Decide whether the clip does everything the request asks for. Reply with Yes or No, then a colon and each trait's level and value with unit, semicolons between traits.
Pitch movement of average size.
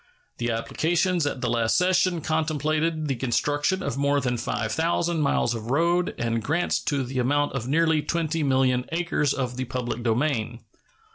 Yes: average, 4.7 semitones